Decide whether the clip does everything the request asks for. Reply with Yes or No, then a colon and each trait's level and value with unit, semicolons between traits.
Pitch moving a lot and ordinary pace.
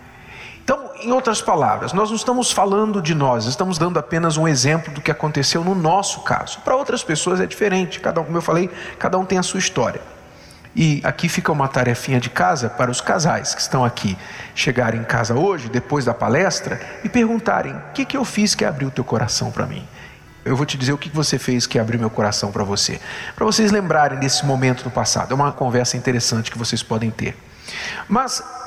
No: wide, 7.2 semitones; fast, 210 wpm